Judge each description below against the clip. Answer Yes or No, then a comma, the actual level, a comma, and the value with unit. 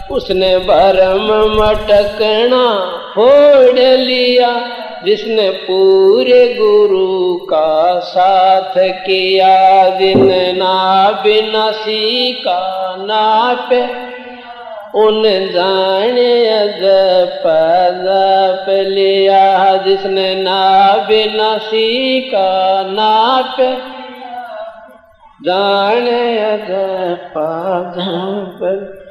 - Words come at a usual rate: No, slow, 60 wpm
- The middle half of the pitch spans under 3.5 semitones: No, average, 4.1 semitones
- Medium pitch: No, high, 200 Hz